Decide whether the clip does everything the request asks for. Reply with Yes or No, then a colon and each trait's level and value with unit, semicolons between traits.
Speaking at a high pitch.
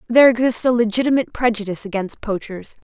Yes: high, 225 Hz